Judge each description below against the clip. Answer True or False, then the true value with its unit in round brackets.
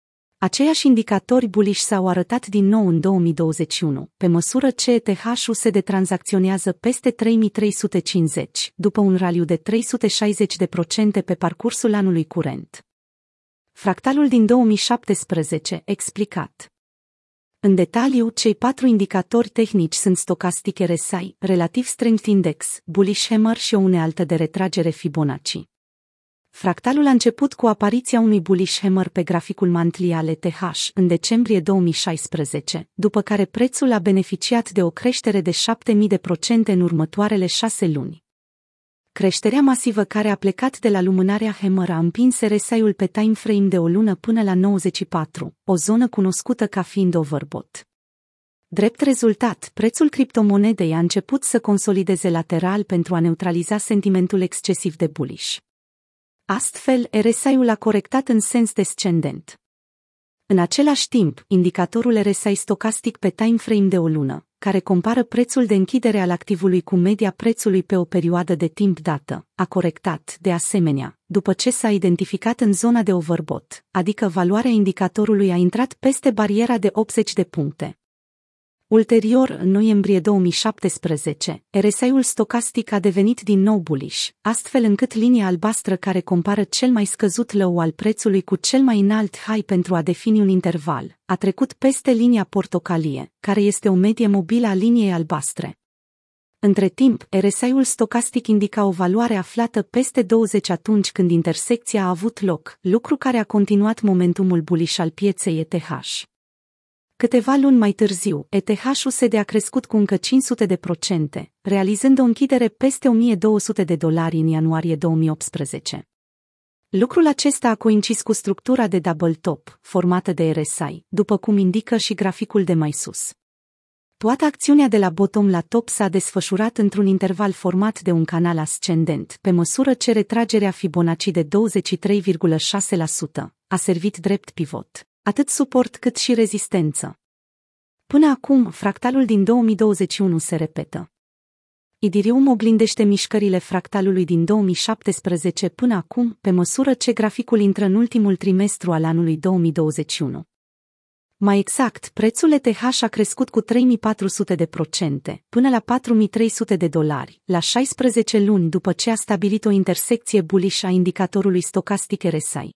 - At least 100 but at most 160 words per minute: True (140 wpm)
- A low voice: False (200 Hz)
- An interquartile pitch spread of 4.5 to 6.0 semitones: False (4.1 semitones)